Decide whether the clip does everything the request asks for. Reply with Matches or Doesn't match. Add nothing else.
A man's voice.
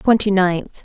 Doesn't match